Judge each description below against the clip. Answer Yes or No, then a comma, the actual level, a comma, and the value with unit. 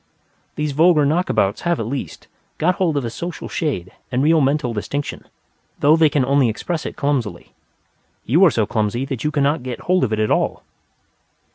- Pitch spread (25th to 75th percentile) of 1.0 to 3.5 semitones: No, average, 4.9 semitones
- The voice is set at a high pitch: No, medium, 140 Hz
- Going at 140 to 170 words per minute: No, average, 185 wpm